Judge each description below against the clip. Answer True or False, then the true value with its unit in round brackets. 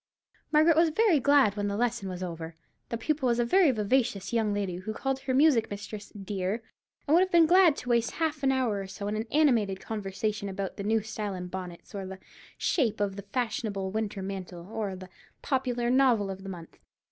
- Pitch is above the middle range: True (215 Hz)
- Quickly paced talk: True (215 wpm)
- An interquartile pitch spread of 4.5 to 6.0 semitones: True (5.2 semitones)